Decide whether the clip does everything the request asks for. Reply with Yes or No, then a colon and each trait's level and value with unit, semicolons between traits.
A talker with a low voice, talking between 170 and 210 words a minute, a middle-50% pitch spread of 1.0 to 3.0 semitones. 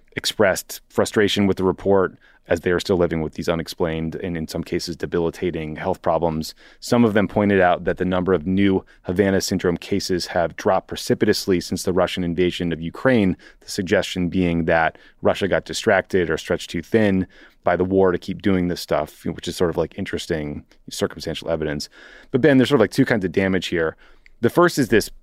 Yes: very low, 90 Hz; average, 200 wpm; average, 2.7 semitones